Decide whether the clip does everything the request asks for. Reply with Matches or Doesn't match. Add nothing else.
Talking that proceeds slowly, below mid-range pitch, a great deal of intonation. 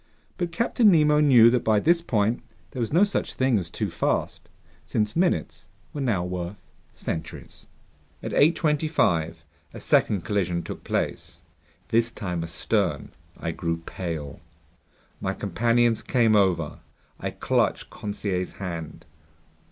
Matches